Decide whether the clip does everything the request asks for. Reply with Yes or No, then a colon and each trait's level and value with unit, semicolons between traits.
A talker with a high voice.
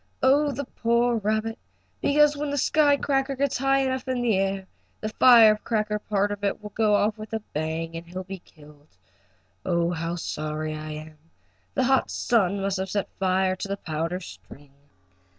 Yes: high, 205 Hz